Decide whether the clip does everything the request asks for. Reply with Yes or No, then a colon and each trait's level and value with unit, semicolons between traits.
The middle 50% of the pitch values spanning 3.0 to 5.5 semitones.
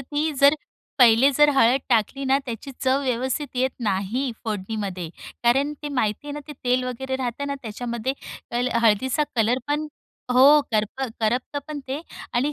Yes: average, 3.5 semitones